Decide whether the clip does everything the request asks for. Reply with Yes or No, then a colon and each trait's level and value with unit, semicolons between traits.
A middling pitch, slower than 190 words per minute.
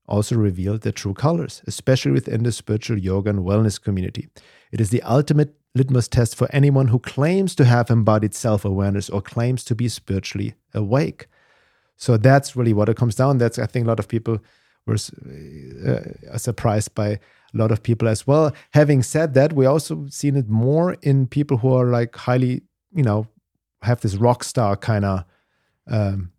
No: low, 120 Hz; average, 180 wpm